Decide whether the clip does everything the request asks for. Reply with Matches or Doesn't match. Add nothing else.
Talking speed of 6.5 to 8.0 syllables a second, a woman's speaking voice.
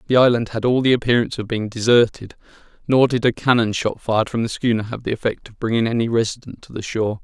Doesn't match